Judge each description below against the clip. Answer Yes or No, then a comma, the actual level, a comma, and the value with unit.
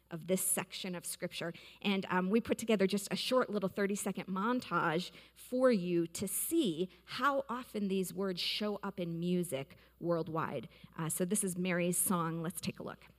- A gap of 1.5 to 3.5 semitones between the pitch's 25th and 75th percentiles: Yes, average, 2.7 semitones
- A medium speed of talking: Yes, average, 180 wpm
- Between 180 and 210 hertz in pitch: Yes, medium, 185 Hz